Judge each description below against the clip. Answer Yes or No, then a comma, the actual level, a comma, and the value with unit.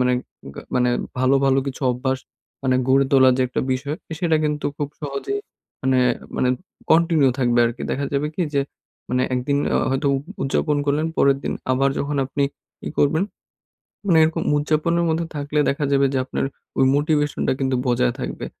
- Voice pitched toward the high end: No, medium, 140 Hz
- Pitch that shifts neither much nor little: No, narrow, 2.3 semitones